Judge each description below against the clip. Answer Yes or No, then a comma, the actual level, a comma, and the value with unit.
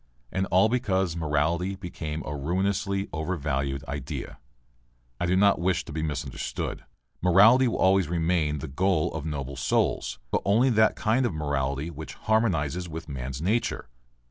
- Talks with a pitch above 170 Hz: No, very low, 85 Hz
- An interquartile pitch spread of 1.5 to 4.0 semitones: No, average, 4.7 semitones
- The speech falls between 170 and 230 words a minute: No, average, 150 wpm